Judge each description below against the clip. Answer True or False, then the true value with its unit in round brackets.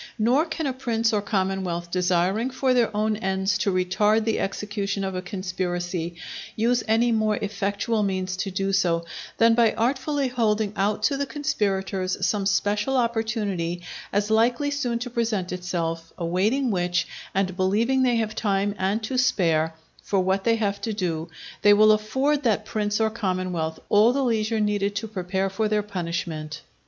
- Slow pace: False (165 wpm)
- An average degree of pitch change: True (3.5 semitones)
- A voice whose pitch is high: True (205 Hz)